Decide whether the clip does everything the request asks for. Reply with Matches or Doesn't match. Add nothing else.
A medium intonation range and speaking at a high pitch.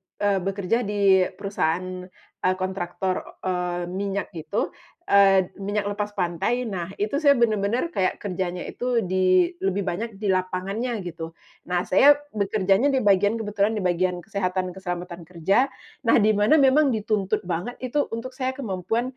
Matches